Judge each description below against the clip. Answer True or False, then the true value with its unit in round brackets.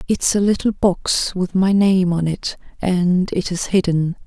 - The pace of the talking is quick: False (185 wpm)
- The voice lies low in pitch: False (185 Hz)